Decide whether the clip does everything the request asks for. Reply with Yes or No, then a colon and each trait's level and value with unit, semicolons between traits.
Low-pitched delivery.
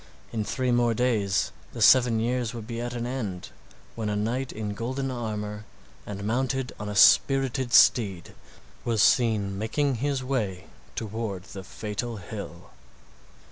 Yes: low, 115 Hz